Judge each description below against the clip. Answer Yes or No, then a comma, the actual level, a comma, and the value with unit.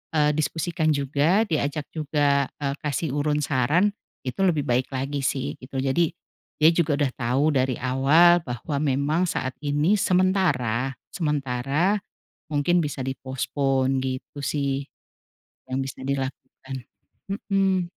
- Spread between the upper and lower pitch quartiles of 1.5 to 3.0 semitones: No, average, 3.4 semitones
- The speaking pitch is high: No, medium, 145 Hz